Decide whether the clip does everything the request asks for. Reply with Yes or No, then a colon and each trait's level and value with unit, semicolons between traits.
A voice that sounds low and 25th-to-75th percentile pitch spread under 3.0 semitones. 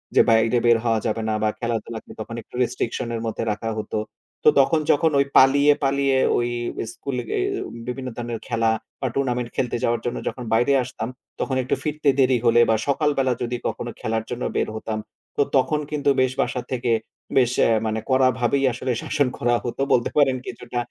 Yes: low, 125 Hz; narrow, 2.6 semitones